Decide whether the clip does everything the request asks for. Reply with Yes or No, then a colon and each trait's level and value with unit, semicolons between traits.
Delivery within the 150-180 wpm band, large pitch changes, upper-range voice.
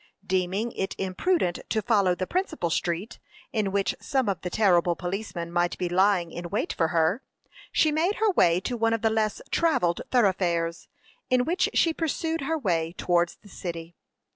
Yes: average, 175 wpm; wide, 5.7 semitones; high, 195 Hz